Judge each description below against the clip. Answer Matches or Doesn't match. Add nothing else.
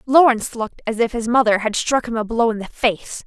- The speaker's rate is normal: Doesn't match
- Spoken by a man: Doesn't match